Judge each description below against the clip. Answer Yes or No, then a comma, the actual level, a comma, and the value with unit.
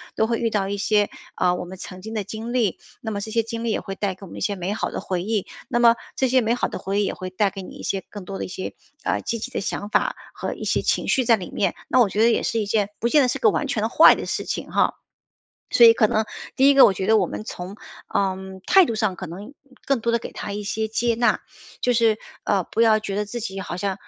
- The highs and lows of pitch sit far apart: No, average, 2.9 semitones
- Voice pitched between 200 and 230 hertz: Yes, high, 215 Hz